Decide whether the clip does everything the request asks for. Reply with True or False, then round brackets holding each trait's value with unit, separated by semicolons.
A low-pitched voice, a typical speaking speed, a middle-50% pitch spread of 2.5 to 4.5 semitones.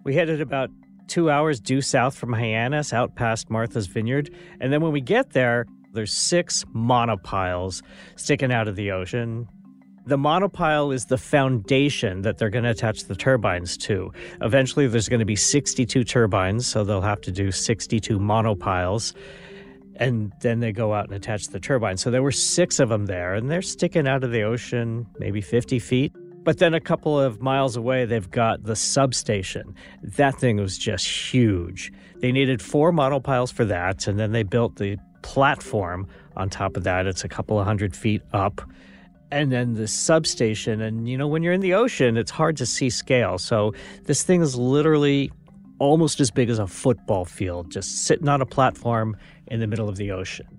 False (120 Hz; 190 wpm; 5.0 semitones)